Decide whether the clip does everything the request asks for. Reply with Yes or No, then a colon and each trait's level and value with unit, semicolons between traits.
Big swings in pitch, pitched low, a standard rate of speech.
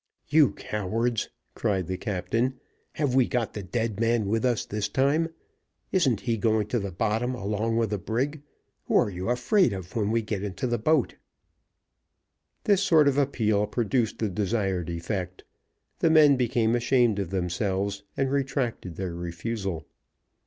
No: average, 4.2 semitones; low, 110 Hz; average, 160 wpm